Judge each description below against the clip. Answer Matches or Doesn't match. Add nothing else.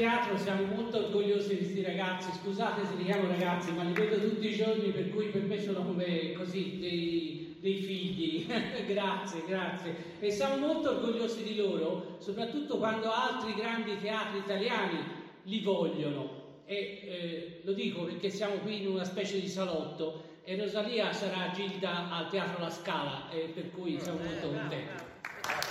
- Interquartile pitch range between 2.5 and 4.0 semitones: Matches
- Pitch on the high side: Matches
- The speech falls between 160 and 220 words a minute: Matches